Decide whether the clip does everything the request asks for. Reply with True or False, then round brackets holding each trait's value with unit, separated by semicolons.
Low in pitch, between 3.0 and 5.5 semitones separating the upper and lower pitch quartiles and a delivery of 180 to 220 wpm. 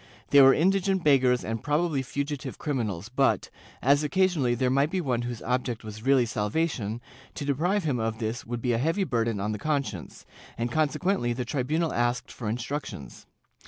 True (130 Hz; 4.4 semitones; 185 wpm)